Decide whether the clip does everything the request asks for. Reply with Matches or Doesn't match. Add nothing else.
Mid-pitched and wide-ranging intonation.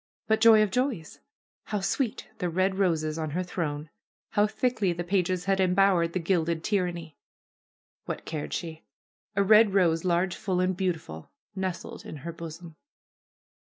Doesn't match